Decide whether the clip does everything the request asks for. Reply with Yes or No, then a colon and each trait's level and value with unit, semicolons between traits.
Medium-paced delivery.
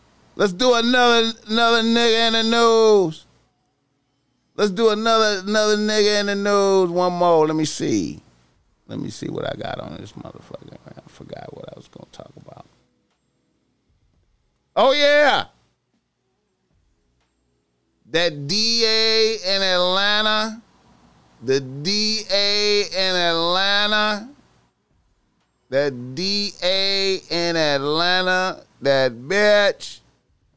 No: slow, 105 wpm